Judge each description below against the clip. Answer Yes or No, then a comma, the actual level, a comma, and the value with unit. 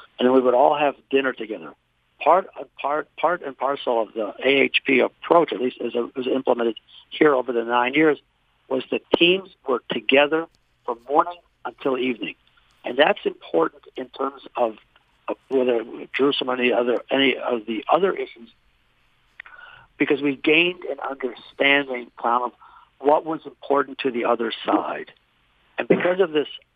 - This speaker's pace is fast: No, average, 160 wpm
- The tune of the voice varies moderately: Yes, average, 4.1 semitones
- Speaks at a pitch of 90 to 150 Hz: Yes, low, 135 Hz